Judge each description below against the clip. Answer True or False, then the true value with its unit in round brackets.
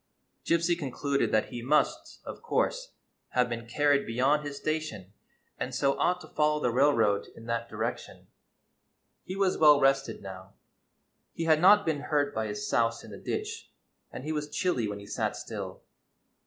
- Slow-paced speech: False (175 wpm)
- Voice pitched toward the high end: False (140 Hz)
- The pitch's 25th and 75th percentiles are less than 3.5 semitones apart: False (5.1 semitones)